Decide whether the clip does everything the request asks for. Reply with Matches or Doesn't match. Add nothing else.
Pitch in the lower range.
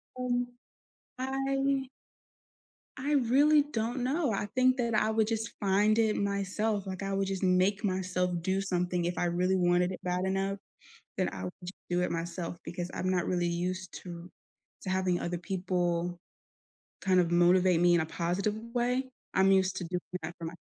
Doesn't match